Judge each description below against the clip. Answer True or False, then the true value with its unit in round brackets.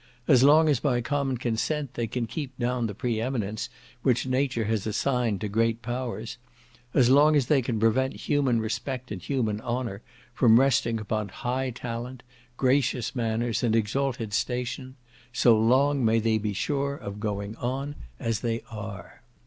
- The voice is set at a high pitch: False (120 Hz)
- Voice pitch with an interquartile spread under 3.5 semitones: True (2.9 semitones)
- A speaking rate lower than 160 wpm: False (165 wpm)